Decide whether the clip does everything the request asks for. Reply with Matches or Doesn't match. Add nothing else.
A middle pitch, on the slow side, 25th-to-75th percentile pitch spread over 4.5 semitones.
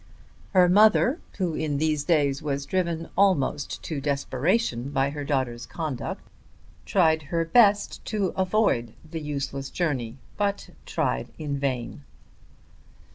Matches